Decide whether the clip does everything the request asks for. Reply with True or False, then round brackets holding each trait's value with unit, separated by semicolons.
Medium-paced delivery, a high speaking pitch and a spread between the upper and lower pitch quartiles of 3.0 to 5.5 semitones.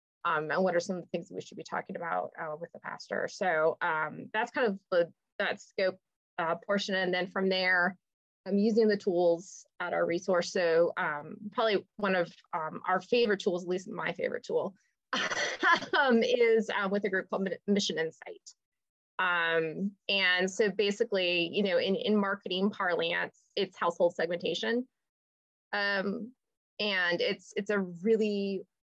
True (165 wpm; 200 Hz; 3.4 semitones)